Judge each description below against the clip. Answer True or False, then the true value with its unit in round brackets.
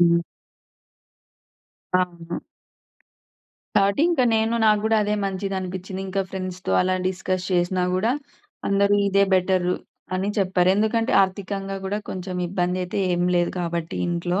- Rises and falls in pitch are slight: True (1.8 semitones)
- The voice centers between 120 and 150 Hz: False (185 Hz)